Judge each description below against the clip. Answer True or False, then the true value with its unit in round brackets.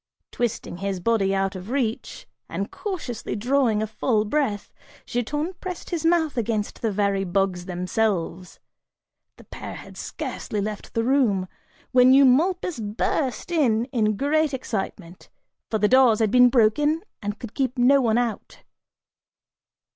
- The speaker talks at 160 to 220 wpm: False (140 wpm)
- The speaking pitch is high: True (230 Hz)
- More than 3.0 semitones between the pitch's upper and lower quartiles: True (4.8 semitones)